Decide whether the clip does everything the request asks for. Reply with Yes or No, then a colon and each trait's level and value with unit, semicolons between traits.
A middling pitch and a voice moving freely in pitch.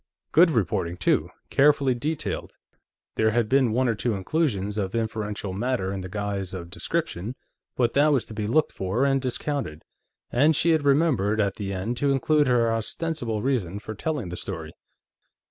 No: low, 115 Hz; wide, 5.7 semitones